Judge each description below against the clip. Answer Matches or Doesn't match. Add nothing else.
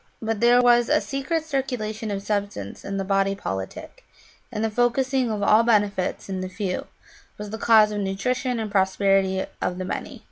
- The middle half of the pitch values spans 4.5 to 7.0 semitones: Doesn't match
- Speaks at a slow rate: Doesn't match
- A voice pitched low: Doesn't match